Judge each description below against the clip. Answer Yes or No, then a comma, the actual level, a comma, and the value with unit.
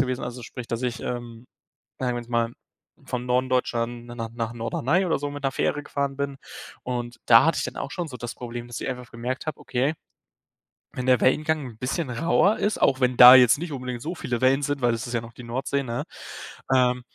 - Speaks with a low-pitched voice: Yes, low, 125 Hz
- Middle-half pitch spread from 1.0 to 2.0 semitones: No, narrow, 2.4 semitones